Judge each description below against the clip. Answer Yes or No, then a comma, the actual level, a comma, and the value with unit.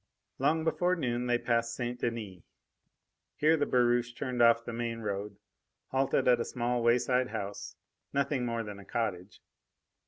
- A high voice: No, low, 120 Hz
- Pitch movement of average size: No, narrow, 1.7 semitones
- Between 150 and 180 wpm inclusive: Yes, average, 155 wpm